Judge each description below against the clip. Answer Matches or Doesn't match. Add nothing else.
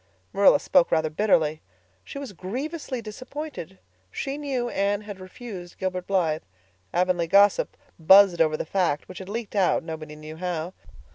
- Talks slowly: Doesn't match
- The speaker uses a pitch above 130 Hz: Matches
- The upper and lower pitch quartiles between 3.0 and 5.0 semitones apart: Doesn't match